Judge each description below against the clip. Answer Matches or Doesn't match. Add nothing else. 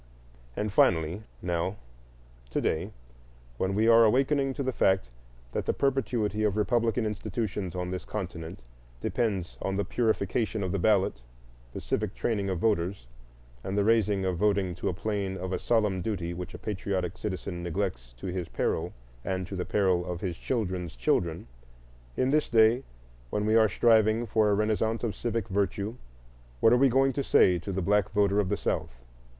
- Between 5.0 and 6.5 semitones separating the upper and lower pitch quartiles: Doesn't match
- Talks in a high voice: Doesn't match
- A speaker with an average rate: Matches